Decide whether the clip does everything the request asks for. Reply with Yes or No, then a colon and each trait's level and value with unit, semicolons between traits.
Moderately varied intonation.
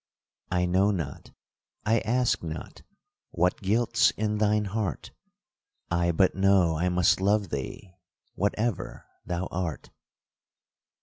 Yes: average, 3.4 semitones